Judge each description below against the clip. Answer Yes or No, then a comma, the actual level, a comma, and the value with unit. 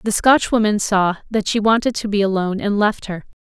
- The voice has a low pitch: No, high, 205 Hz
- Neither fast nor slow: No, fast, 210 wpm